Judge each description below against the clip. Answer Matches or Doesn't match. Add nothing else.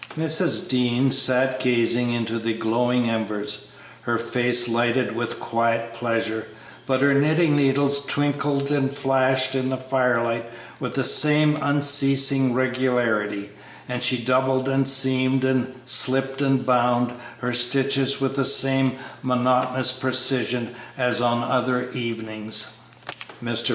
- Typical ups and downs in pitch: Doesn't match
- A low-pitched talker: Matches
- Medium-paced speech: Doesn't match